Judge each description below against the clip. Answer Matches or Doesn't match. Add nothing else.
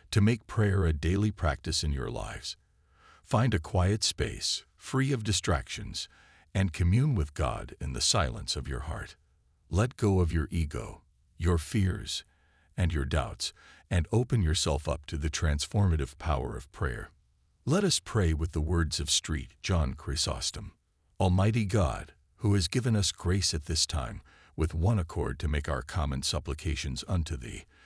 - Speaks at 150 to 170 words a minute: Matches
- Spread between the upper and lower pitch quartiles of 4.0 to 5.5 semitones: Matches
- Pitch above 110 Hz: Doesn't match